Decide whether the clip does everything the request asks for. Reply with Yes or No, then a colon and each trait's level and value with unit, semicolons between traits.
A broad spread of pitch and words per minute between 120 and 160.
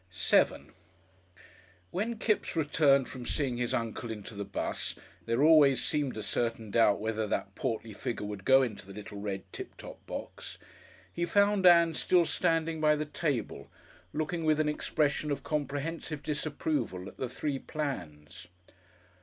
Yes: wide, 5.8 semitones; average, 155 wpm